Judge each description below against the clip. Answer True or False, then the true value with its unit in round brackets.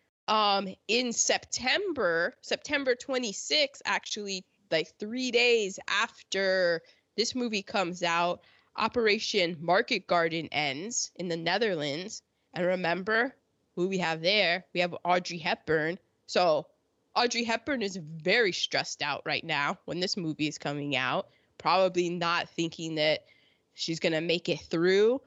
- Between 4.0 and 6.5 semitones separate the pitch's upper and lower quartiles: True (4.4 semitones)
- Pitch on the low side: False (180 Hz)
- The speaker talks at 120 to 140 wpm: True (135 wpm)